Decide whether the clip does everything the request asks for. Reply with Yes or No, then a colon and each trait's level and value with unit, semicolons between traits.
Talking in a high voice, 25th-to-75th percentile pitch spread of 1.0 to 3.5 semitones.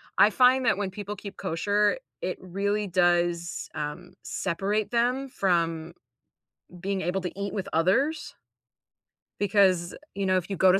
Yes: high, 195 Hz; average, 2.7 semitones